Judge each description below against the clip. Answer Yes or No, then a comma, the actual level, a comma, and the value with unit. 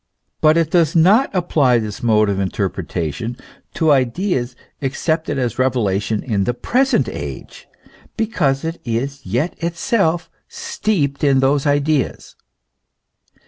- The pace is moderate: No, slow, 125 wpm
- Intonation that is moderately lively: No, wide, 5.7 semitones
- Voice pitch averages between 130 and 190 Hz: Yes, medium, 140 Hz